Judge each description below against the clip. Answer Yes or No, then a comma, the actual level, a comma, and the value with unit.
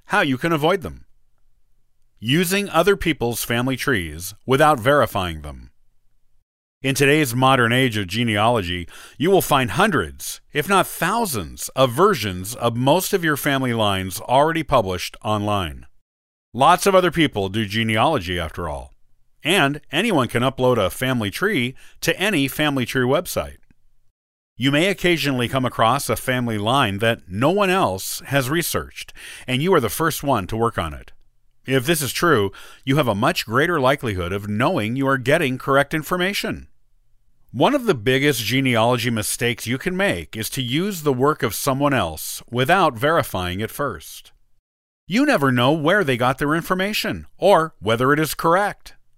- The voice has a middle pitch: No, low, 130 Hz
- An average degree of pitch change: No, wide, 5.9 semitones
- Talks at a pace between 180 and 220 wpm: No, average, 160 wpm